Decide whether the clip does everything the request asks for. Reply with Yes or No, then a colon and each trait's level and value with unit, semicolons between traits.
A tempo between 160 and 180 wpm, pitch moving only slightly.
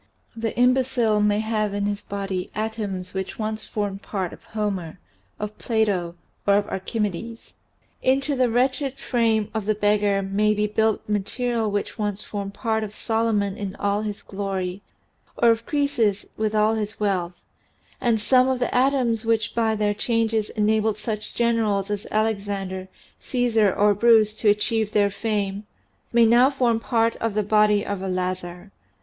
Yes: average, 165 wpm; narrow, 2.1 semitones